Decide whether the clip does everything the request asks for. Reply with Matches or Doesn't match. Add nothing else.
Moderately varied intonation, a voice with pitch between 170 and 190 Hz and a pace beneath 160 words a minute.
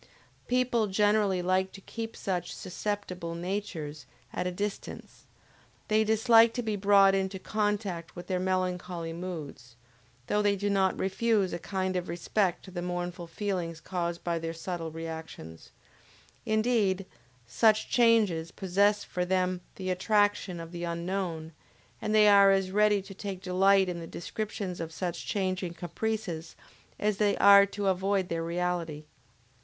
Matches